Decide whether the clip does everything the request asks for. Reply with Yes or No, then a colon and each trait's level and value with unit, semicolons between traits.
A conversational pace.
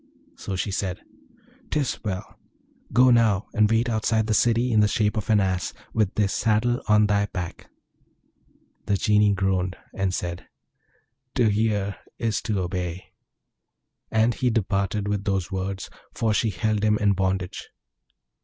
Yes: average, 150 wpm